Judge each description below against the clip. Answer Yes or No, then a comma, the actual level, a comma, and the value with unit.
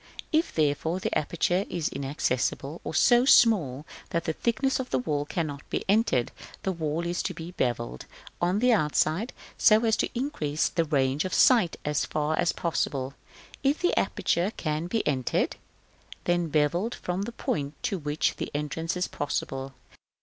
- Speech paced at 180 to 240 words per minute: No, average, 165 wpm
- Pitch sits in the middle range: Yes, medium, 165 Hz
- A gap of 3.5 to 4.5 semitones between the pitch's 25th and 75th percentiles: No, average, 5.2 semitones